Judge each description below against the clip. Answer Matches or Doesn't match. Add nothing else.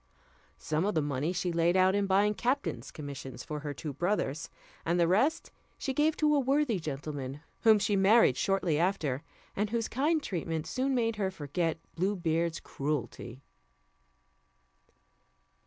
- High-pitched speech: Doesn't match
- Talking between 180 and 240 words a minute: Doesn't match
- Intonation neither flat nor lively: Doesn't match